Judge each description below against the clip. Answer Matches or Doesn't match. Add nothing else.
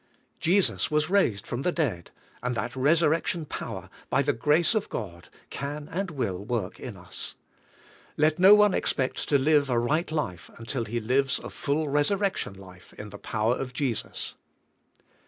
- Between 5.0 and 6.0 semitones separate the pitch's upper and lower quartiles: Matches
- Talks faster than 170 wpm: Doesn't match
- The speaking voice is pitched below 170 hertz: Matches